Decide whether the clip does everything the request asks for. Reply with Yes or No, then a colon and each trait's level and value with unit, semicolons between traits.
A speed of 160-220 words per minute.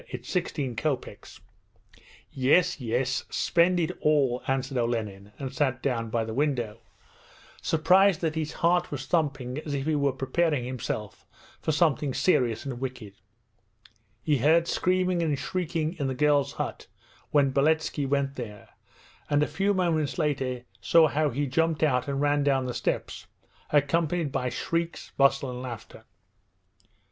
No: average, 150 wpm